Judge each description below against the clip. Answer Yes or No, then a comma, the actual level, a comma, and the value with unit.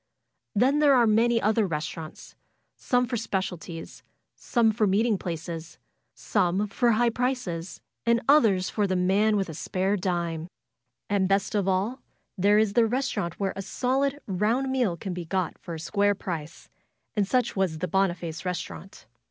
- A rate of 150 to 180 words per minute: Yes, average, 160 wpm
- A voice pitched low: No, high, 195 Hz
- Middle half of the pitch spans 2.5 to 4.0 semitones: No, average, 4.5 semitones